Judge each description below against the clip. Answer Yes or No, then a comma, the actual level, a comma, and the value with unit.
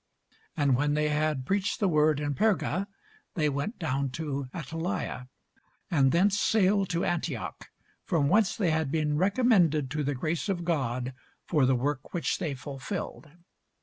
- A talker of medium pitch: Yes, medium, 155 Hz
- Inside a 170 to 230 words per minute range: No, average, 155 wpm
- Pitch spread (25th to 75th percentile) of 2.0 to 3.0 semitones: No, average, 4.3 semitones